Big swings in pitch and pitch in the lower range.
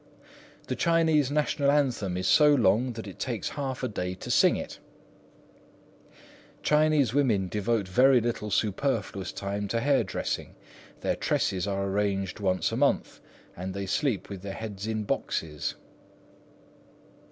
Yes: wide, 5.7 semitones; low, 105 Hz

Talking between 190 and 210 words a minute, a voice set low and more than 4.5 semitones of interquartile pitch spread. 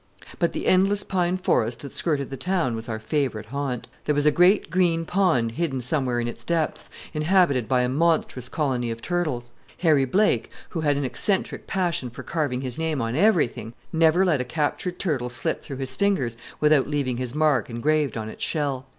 No: average, 195 wpm; medium, 145 Hz; average, 5.2 semitones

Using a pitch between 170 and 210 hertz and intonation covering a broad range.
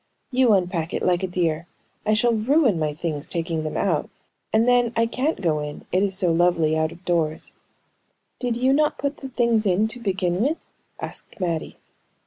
Yes: high, 190 Hz; wide, 6.0 semitones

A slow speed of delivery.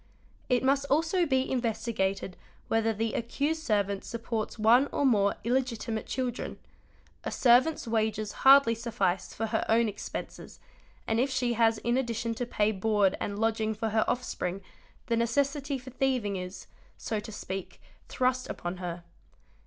No: average, 160 wpm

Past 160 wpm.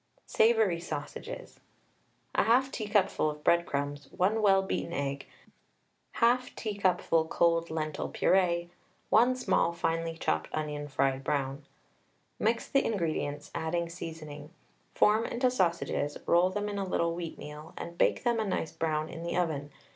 No: slow, 135 wpm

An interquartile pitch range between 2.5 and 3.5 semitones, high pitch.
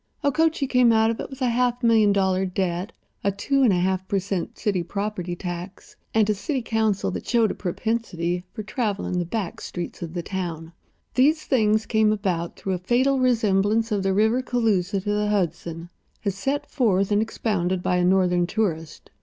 No: average, 4.0 semitones; high, 205 Hz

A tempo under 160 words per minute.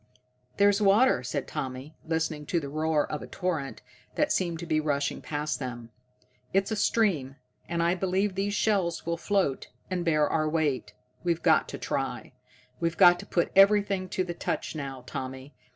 No: average, 175 wpm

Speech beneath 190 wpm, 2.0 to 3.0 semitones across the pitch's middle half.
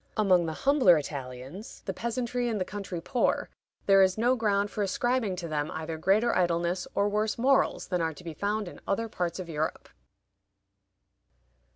No: average, 175 wpm; average, 4.4 semitones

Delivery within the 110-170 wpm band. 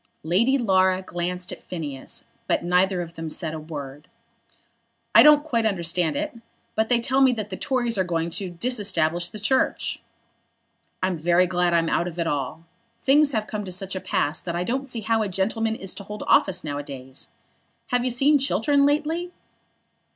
No: average, 190 wpm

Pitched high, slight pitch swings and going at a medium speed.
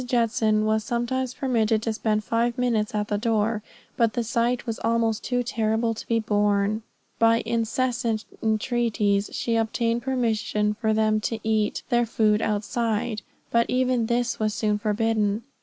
Yes: high, 225 Hz; narrow, 1.7 semitones; average, 155 wpm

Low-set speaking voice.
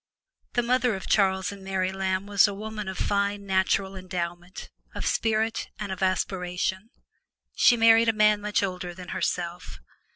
No: high, 195 Hz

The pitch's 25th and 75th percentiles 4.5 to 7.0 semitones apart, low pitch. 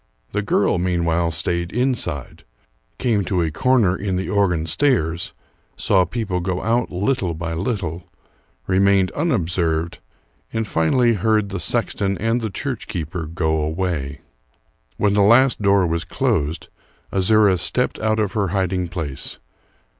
No: average, 4.0 semitones; very low, 95 Hz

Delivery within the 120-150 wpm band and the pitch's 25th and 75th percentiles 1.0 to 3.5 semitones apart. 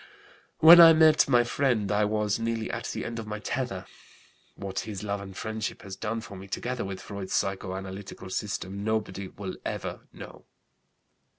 No: average, 170 wpm; average, 2.9 semitones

